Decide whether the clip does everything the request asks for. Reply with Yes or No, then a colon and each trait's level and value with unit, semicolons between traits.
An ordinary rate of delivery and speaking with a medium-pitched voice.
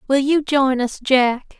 No: average, 190 wpm; very high, 265 Hz